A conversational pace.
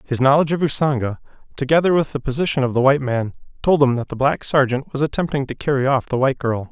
No: fast, 230 wpm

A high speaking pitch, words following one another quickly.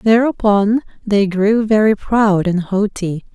No: high, 205 Hz; slow, 125 wpm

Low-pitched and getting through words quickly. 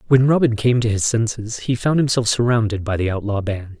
Yes: low, 115 Hz; fast, 220 wpm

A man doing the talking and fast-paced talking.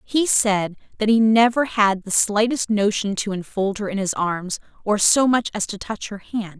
No: female; fast, 210 wpm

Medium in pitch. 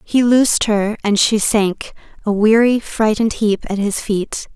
No: high, 215 Hz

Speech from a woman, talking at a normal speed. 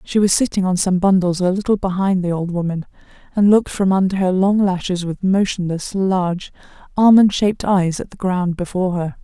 Yes: female; average, 195 wpm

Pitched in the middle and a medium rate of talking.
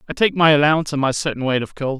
No: medium, 145 Hz; fast, 300 wpm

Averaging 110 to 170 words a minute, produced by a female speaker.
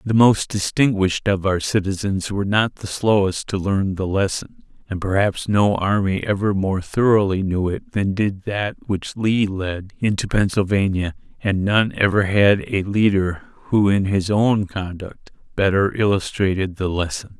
No: average, 160 wpm; male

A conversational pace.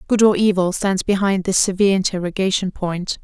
Yes: average, 165 wpm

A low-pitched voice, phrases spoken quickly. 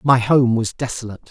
No: low, 120 Hz; average, 185 wpm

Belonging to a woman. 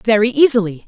Yes: female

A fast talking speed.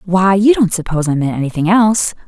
Yes: fast, 210 wpm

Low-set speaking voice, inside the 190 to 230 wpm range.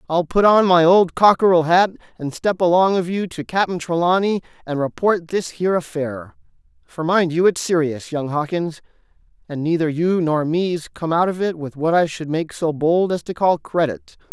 No: medium, 170 Hz; average, 195 wpm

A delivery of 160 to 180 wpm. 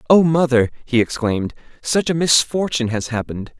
No: average, 150 wpm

